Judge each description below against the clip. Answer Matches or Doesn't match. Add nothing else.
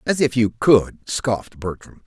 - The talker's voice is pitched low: Matches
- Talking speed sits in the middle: Matches